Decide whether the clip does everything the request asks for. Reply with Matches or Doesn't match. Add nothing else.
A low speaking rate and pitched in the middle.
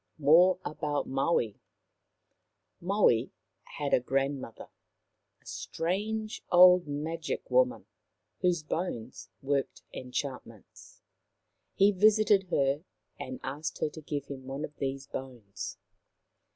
Matches